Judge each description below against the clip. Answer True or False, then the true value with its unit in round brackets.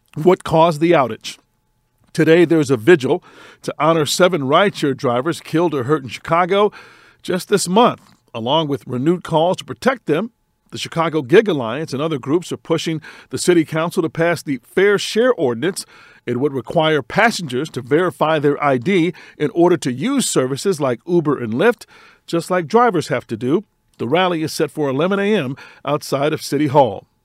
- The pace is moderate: True (175 wpm)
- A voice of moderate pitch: True (160 Hz)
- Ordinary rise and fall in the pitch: True (4.3 semitones)